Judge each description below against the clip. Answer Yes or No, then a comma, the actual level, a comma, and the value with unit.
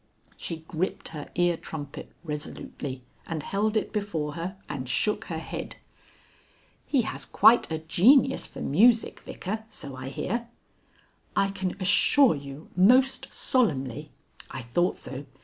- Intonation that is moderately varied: No, wide, 6.6 semitones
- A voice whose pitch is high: No, medium, 175 Hz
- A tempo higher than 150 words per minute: No, average, 140 wpm